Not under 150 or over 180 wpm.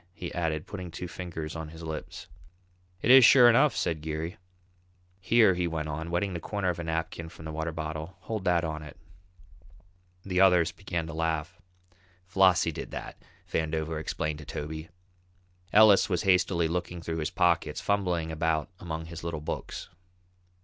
Yes: average, 165 wpm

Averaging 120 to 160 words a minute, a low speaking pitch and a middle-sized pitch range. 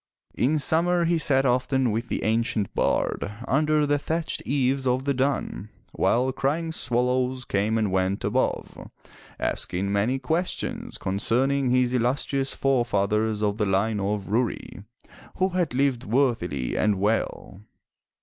Yes: average, 140 wpm; low, 125 Hz; average, 4.5 semitones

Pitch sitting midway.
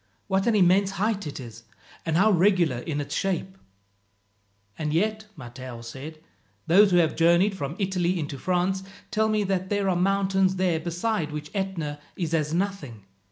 Yes: medium, 180 Hz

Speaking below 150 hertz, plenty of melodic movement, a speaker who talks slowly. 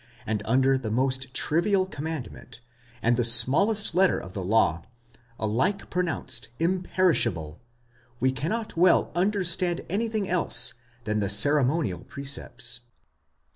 Yes: low, 135 Hz; wide, 7.6 semitones; slow, 115 wpm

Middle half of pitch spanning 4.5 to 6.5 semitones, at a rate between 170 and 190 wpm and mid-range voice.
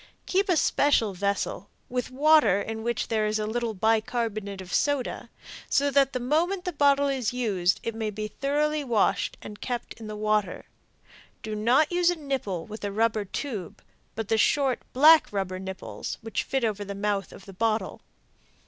No: average, 5.0 semitones; average, 180 wpm; high, 225 Hz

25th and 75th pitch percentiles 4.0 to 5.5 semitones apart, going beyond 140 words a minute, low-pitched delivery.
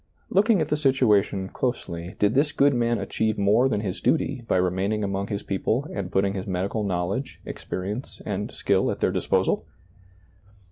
Yes: average, 4.8 semitones; average, 175 wpm; low, 105 Hz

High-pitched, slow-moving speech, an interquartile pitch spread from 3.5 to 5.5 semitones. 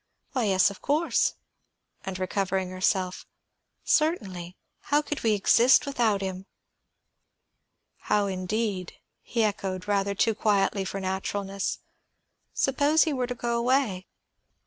Yes: high, 200 Hz; slow, 120 wpm; average, 4.3 semitones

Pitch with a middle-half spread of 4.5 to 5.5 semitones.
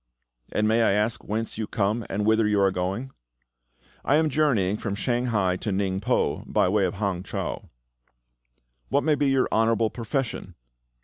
No: average, 3.6 semitones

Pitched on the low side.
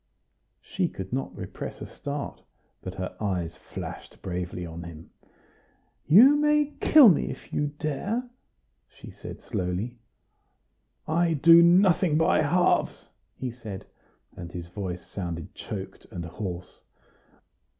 Yes: low, 120 Hz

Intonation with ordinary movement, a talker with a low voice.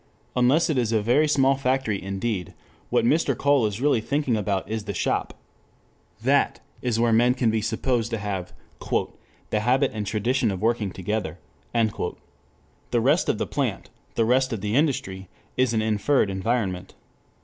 Yes: average, 3.7 semitones; low, 115 Hz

